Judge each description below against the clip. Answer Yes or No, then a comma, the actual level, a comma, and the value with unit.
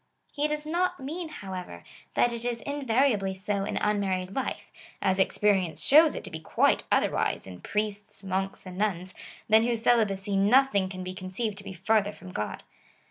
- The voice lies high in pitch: Yes, high, 205 Hz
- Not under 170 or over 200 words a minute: Yes, average, 180 wpm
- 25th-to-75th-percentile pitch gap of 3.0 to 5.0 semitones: Yes, average, 4.1 semitones